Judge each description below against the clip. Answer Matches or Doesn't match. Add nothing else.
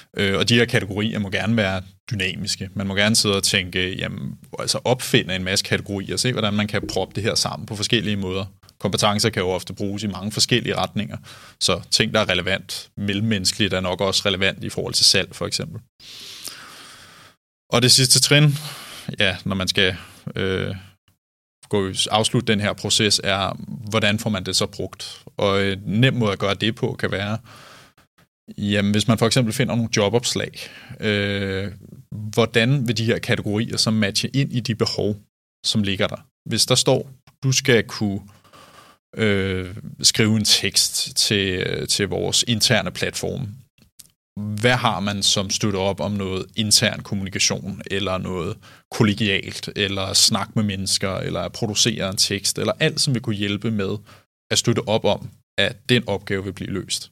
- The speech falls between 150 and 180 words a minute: Matches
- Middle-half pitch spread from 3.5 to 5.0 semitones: Doesn't match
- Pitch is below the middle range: Matches